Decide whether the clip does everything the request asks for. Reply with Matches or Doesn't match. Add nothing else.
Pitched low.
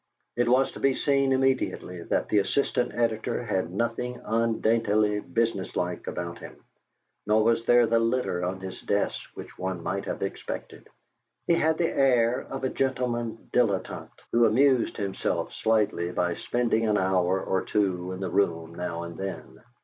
Matches